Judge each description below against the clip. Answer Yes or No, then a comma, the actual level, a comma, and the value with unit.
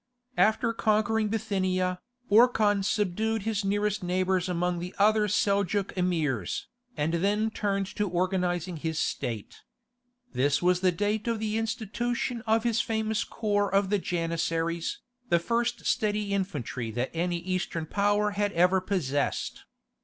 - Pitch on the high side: Yes, high, 195 Hz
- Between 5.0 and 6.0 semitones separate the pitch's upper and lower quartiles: No, average, 3.4 semitones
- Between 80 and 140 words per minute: Yes, slow, 135 wpm